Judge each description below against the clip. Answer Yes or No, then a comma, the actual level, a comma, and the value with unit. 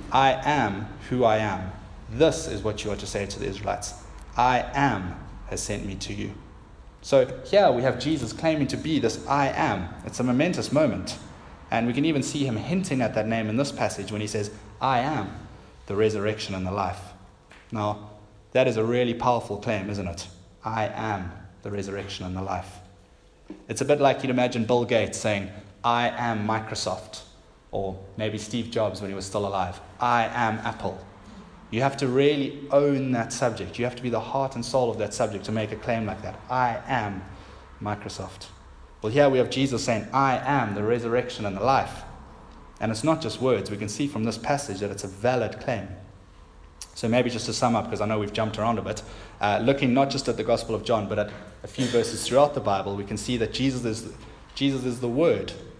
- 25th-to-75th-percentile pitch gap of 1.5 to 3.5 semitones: No, average, 3.9 semitones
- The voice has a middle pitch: No, low, 110 Hz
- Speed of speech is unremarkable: No, fast, 210 wpm